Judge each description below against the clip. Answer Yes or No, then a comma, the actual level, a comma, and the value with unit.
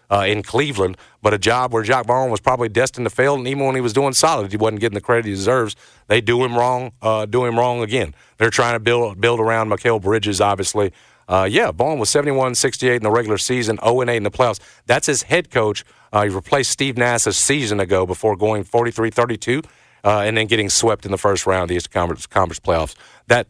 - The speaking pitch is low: Yes, low, 115 Hz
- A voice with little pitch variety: No, average, 3.2 semitones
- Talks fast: Yes, fast, 230 wpm